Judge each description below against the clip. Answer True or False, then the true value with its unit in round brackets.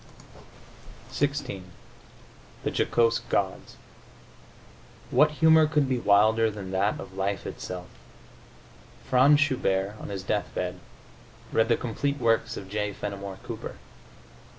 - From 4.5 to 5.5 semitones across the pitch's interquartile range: True (4.8 semitones)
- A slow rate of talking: True (110 wpm)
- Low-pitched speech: True (110 Hz)